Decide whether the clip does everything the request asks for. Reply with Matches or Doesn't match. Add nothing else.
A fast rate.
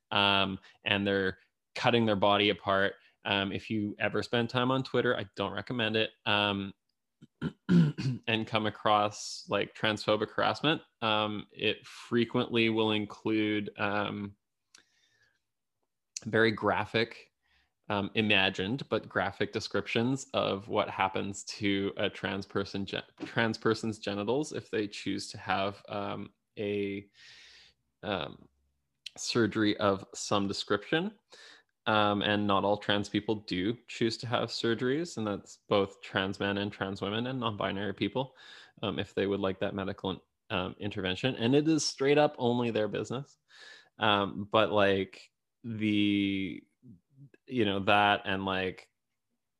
Doesn't match